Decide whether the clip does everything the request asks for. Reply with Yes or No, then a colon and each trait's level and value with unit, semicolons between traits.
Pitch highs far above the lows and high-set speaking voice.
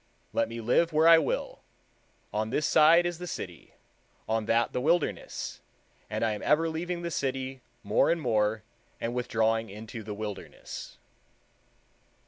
No: wide, 6.6 semitones; low, 125 Hz